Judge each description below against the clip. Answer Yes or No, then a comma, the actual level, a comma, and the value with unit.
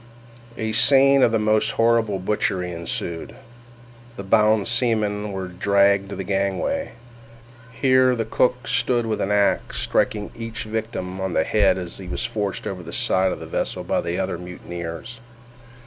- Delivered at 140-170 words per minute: Yes, average, 165 wpm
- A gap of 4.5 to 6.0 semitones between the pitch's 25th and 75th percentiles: No, average, 3.3 semitones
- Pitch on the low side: Yes, low, 105 Hz